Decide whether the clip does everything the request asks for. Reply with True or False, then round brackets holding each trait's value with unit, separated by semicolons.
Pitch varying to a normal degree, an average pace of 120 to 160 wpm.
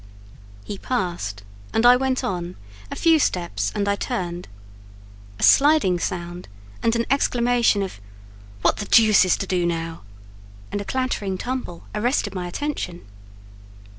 False (5.7 semitones; 140 wpm)